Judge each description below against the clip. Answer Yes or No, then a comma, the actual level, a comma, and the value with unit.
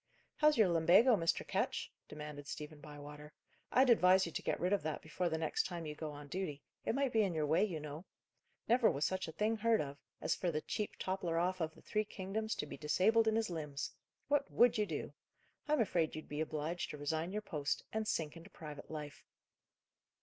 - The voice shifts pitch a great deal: Yes, wide, 5.8 semitones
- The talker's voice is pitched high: No, medium, 170 Hz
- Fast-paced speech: Yes, fast, 215 wpm